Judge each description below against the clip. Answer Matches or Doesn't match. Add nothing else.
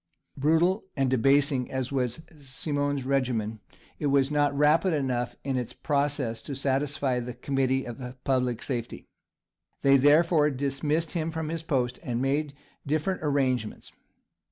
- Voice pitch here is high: Doesn't match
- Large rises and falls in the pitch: Doesn't match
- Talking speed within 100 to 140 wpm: Matches